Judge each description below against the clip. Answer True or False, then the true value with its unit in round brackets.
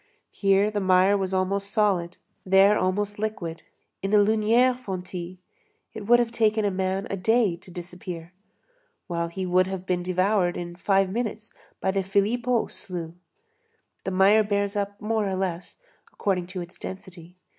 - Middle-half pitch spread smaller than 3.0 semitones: True (2.4 semitones)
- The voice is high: True (195 Hz)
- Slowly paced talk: False (160 wpm)